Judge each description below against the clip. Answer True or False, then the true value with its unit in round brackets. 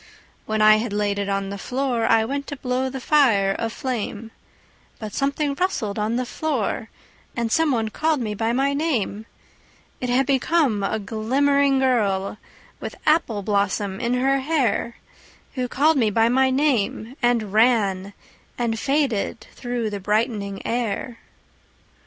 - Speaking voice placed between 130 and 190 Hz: False (235 Hz)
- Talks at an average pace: True (150 wpm)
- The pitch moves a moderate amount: True (4.3 semitones)